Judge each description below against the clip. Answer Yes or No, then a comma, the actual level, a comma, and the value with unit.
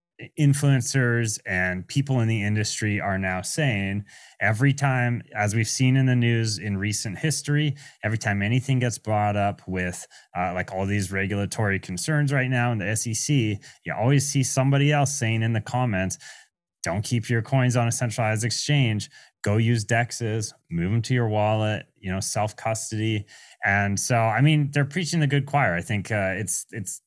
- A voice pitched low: Yes, low, 115 Hz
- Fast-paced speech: No, average, 180 wpm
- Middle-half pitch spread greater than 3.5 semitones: Yes, average, 4.2 semitones